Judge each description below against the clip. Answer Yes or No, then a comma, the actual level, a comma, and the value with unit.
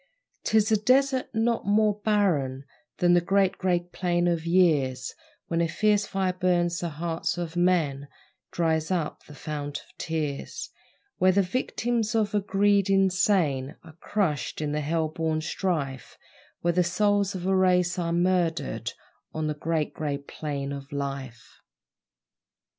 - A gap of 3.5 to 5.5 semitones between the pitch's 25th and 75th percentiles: Yes, average, 4.1 semitones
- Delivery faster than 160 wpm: No, average, 150 wpm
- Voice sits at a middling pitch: Yes, medium, 175 Hz